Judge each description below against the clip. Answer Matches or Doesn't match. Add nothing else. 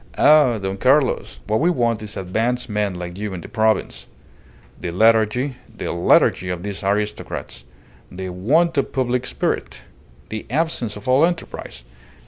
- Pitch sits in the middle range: Doesn't match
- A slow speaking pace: Doesn't match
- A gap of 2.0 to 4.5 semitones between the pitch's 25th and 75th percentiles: Doesn't match